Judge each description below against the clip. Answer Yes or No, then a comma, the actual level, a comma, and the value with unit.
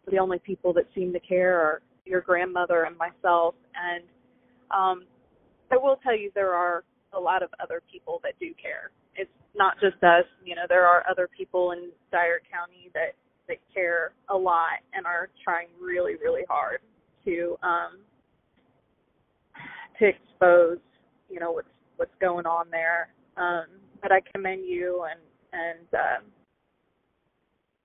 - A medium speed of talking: Yes, average, 155 wpm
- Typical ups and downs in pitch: No, narrow, 2.2 semitones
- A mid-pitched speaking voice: Yes, medium, 180 Hz